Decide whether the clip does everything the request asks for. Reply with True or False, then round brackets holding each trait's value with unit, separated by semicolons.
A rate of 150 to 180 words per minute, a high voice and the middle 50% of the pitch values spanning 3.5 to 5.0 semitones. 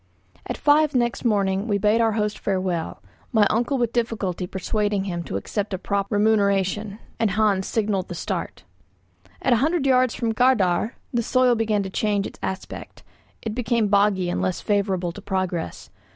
False (170 wpm; 210 Hz; 3.1 semitones)